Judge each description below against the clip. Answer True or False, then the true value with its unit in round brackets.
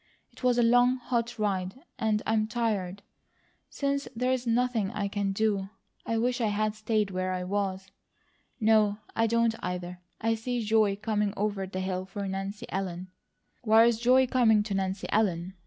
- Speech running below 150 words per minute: False (170 wpm)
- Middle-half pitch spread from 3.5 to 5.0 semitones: False (3.0 semitones)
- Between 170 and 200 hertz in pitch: False (215 Hz)